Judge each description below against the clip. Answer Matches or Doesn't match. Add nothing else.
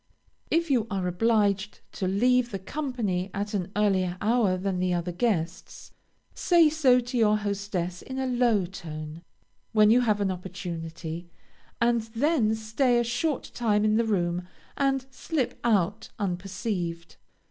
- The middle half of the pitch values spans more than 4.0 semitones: Matches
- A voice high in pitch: Matches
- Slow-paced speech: Doesn't match